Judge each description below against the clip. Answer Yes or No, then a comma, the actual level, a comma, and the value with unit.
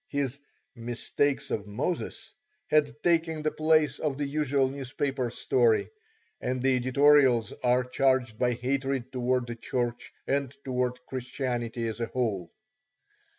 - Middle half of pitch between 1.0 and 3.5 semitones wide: Yes, average, 2.7 semitones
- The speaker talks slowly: Yes, slow, 130 wpm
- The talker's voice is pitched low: Yes, low, 130 Hz